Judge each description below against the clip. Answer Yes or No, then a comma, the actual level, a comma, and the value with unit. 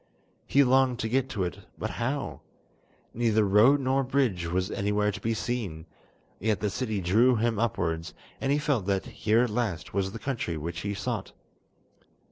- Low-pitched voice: Yes, low, 110 Hz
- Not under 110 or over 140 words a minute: No, average, 175 wpm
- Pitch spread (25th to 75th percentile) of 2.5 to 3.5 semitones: No, average, 4.6 semitones